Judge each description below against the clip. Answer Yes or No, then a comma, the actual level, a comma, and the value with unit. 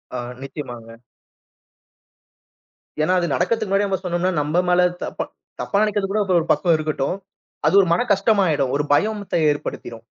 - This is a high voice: No, medium, 180 Hz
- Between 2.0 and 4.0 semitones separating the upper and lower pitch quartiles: No, average, 5.2 semitones